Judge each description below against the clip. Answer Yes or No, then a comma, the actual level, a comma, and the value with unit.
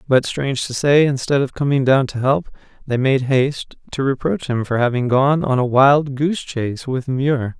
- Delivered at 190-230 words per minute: Yes, fast, 205 wpm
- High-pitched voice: No, low, 135 Hz